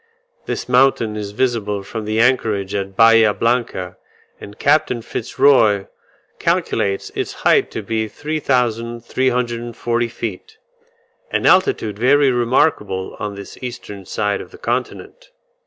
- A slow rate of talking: Yes, slow, 125 wpm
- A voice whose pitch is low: Yes, low, 115 Hz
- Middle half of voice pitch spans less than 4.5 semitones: Yes, average, 3.4 semitones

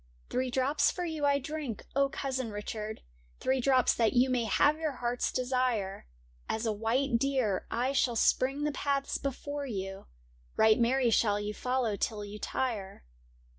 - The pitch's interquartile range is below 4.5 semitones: Yes, average, 3.9 semitones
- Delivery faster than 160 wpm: Yes, average, 170 wpm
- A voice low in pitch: No, very high, 250 Hz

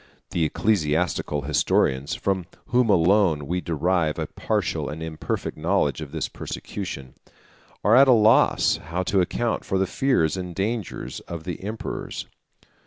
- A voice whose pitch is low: Yes, very low, 90 Hz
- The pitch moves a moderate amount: Yes, average, 4.4 semitones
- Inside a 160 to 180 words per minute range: No, average, 145 wpm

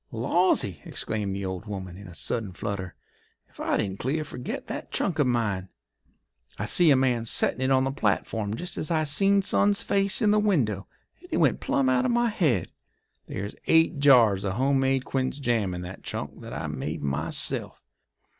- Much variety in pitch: Yes, wide, 7.4 semitones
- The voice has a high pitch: No, low, 125 Hz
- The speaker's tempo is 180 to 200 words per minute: Yes, average, 195 wpm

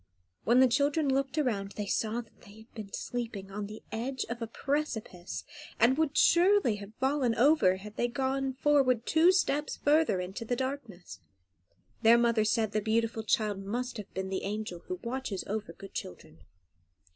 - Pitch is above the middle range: Yes, high, 230 Hz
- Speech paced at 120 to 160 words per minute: No, average, 175 wpm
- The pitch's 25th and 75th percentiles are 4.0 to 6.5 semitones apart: Yes, average, 4.3 semitones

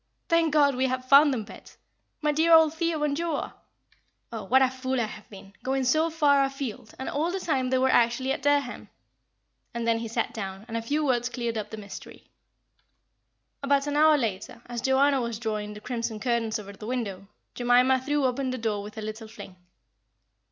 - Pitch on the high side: Yes, very high, 255 Hz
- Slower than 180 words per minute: No, average, 200 wpm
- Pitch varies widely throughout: No, average, 4.1 semitones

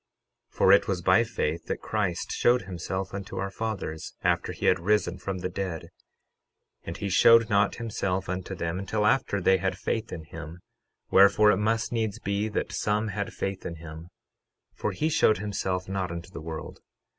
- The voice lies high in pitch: No, very low, 95 Hz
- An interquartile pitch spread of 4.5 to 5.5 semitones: No, average, 3.0 semitones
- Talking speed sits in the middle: Yes, average, 185 wpm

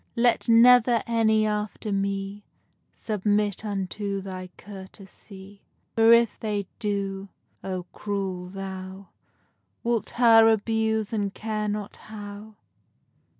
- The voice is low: No, high, 205 Hz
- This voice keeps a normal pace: No, slow, 105 wpm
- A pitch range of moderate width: No, narrow, 2.1 semitones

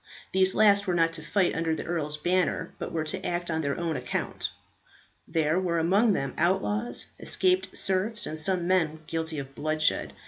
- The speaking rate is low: No, average, 180 wpm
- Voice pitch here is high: No, medium, 170 Hz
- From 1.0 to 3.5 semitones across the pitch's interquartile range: Yes, average, 3.2 semitones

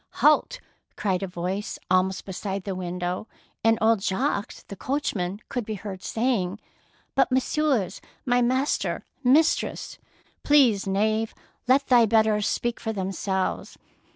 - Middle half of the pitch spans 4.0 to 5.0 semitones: Yes, average, 4.4 semitones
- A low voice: No, high, 215 Hz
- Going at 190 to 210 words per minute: No, average, 155 wpm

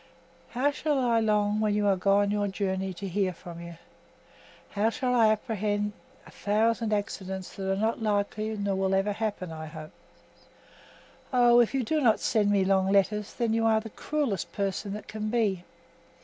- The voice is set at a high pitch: Yes, high, 210 Hz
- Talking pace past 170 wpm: Yes, average, 180 wpm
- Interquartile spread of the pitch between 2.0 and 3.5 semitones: Yes, narrow, 2.4 semitones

